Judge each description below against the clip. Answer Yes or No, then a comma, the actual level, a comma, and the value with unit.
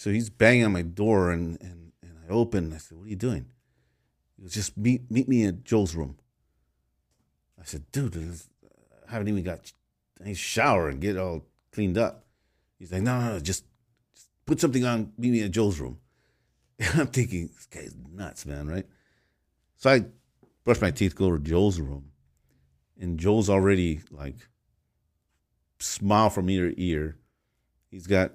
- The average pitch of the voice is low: Yes, very low, 95 Hz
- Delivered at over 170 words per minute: Yes, average, 180 wpm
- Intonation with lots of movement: Yes, wide, 6.4 semitones